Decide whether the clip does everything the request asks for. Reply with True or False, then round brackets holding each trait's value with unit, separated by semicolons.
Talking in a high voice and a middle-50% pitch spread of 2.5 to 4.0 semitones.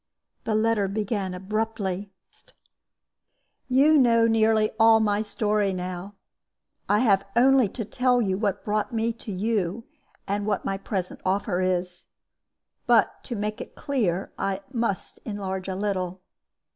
True (205 Hz; 2.8 semitones)